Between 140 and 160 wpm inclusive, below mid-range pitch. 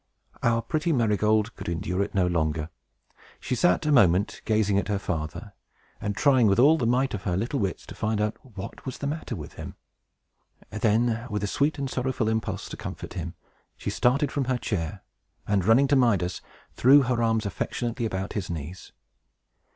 No: average, 185 wpm; low, 110 Hz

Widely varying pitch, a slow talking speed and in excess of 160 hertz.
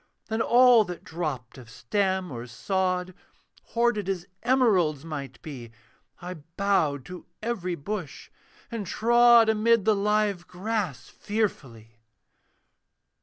Yes: wide, 6.1 semitones; slow, 115 wpm; medium, 185 Hz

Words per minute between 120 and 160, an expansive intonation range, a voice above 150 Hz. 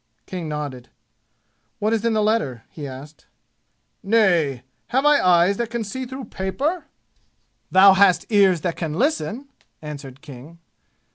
Yes: average, 140 wpm; wide, 7.1 semitones; high, 190 Hz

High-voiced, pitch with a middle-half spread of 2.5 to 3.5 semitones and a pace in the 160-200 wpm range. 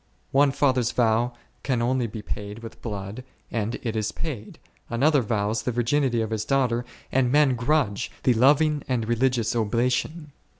No: low, 120 Hz; average, 3.1 semitones; average, 165 wpm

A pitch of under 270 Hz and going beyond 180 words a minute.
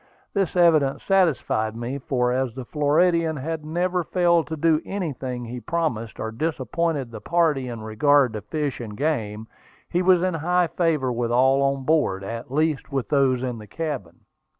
No: medium, 140 Hz; average, 175 wpm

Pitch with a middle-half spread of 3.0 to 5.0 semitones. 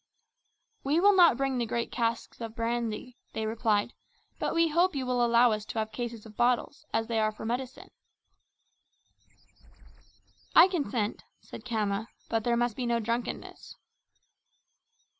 No: narrow, 2.4 semitones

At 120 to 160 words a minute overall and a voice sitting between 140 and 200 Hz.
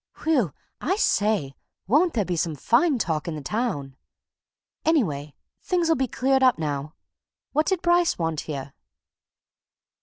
No: average, 140 wpm; high, 215 Hz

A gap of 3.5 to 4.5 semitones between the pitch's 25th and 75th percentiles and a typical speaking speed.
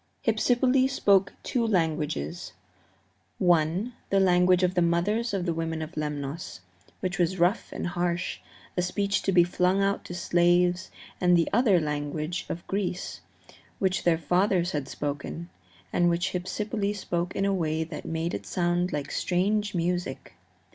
No: average, 2.7 semitones; average, 155 wpm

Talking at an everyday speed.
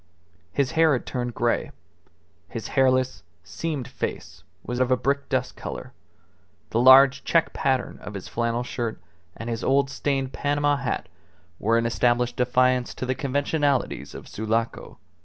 Yes: average, 150 wpm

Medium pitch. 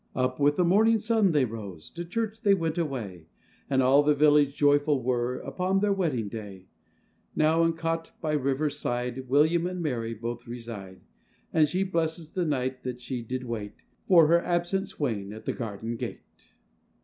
Yes: medium, 145 Hz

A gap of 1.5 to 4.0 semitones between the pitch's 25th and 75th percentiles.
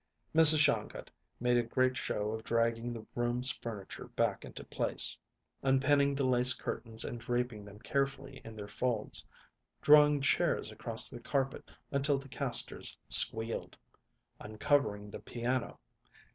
Yes: average, 3.3 semitones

